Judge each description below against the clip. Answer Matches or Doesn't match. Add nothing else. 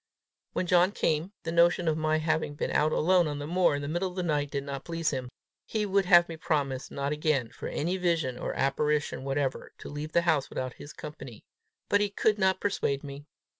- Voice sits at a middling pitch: Matches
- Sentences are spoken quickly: Matches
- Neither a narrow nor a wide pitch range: Matches